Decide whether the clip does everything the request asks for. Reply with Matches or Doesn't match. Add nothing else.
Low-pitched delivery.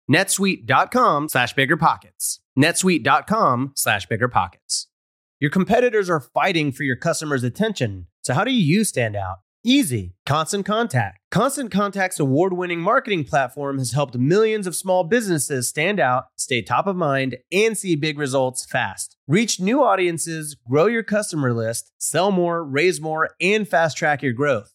Doesn't match